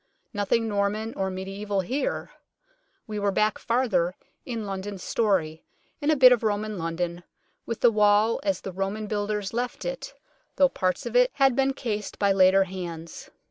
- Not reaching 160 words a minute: No, average, 165 wpm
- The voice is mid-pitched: No, high, 205 Hz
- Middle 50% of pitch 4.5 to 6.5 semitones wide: No, average, 3.3 semitones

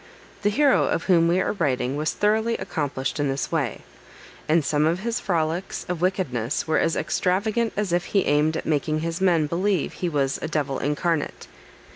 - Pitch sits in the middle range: Yes, medium, 165 Hz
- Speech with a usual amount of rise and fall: Yes, average, 4.3 semitones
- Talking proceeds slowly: No, average, 185 wpm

